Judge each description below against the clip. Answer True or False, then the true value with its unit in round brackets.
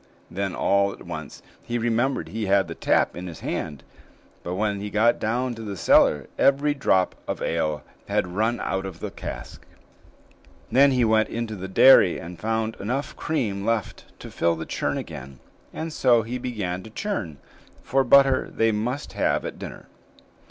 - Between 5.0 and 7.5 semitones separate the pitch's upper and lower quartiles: False (4.6 semitones)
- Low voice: True (110 Hz)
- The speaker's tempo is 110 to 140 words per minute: False (175 wpm)